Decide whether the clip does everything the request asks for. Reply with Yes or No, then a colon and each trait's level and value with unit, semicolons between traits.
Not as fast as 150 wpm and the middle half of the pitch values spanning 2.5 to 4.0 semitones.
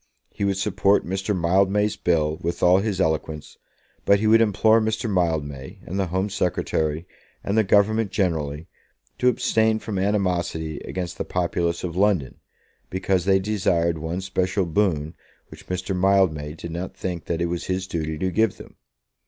No: average, 165 wpm; average, 3.0 semitones